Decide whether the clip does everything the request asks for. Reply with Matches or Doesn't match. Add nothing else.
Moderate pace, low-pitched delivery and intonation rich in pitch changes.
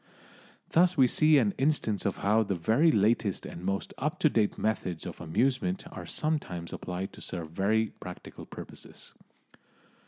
Matches